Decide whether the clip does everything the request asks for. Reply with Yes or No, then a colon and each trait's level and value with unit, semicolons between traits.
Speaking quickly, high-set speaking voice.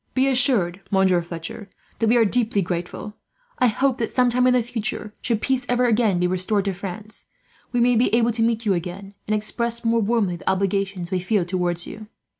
Yes: fast, 210 wpm; high, 215 Hz